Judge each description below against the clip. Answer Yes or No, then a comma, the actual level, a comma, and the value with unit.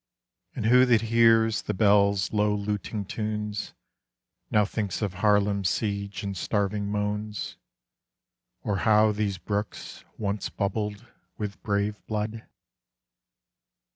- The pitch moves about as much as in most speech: No, narrow, 1.1 semitones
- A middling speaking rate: No, slow, 110 wpm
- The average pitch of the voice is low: Yes, low, 105 Hz